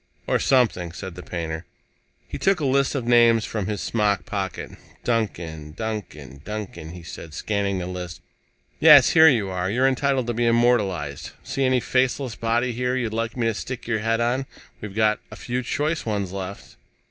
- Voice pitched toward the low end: Yes, low, 110 Hz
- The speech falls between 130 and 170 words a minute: No, average, 180 wpm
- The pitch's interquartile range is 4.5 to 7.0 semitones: Yes, average, 5.0 semitones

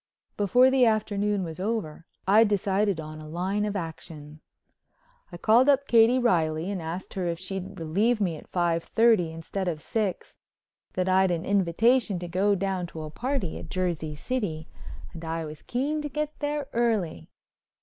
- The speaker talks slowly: No, average, 170 wpm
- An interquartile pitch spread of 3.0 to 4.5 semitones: No, average, 5.1 semitones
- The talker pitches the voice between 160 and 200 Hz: Yes, high, 190 Hz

